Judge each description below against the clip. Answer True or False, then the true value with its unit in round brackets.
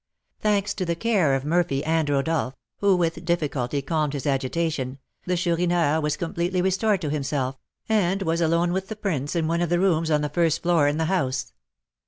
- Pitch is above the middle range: False (165 Hz)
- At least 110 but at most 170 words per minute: False (195 wpm)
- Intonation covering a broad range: False (3.3 semitones)